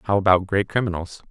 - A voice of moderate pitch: No, very low, 95 Hz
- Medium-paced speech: Yes, average, 185 wpm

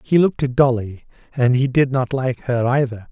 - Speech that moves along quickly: Yes, fast, 210 wpm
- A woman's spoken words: No, male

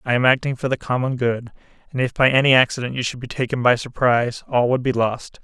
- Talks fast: Yes, fast, 245 wpm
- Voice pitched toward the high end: No, low, 125 Hz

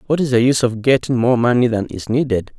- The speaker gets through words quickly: Yes, fast, 255 wpm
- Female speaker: No, male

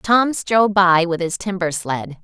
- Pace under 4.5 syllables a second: Yes, 4.1 syllables/s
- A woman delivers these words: Yes, female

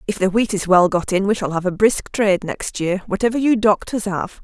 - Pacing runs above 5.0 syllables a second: Yes, 5.4 syllables/s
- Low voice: No, high, 200 Hz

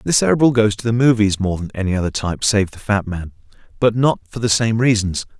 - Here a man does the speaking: Yes, male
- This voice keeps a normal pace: No, fast, 235 wpm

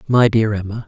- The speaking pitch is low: Yes, low, 110 Hz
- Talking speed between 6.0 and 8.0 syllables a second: No, 5.6 syllables/s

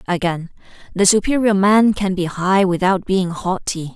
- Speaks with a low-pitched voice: No, high, 190 Hz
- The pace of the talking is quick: No, average, 150 wpm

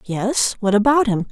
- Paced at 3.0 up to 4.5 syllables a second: Yes, 4.4 syllables/s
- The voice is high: Yes, high, 225 Hz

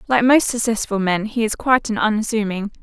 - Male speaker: No, female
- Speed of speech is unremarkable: Yes, average, 190 wpm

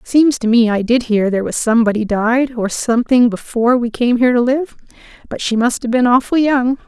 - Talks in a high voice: Yes, high, 240 Hz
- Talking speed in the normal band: No, fast, 220 wpm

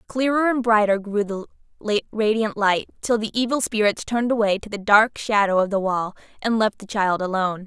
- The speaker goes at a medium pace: Yes, average, 195 wpm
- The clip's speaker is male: No, female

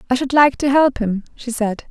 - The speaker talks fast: Yes, fast, 250 wpm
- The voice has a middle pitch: No, very high, 250 Hz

